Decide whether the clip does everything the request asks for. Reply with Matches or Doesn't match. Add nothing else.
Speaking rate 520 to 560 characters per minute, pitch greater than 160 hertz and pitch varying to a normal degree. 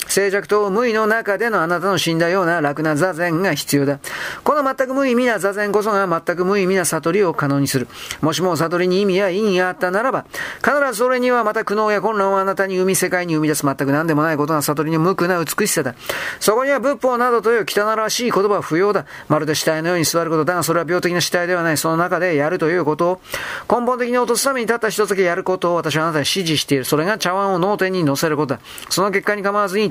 Doesn't match